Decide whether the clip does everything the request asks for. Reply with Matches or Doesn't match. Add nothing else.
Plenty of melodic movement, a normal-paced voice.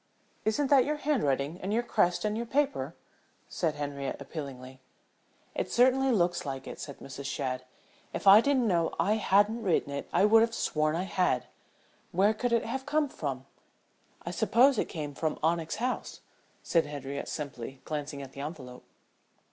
Matches